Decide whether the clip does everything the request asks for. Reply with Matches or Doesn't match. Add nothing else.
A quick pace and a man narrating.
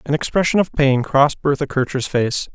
Doesn't match